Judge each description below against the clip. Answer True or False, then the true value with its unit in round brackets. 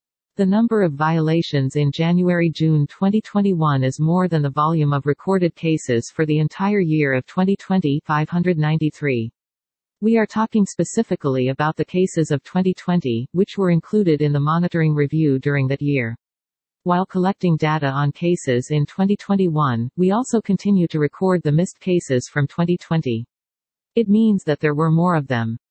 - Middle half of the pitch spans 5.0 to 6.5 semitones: False (4.1 semitones)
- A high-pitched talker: False (160 Hz)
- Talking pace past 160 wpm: False (155 wpm)